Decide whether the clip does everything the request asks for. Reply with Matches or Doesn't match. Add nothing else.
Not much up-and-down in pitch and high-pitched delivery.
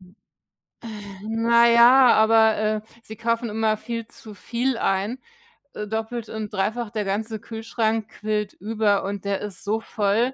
Matches